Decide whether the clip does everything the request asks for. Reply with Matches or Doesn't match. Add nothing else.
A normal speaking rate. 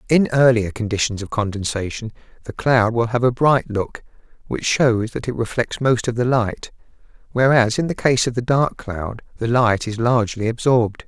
Matches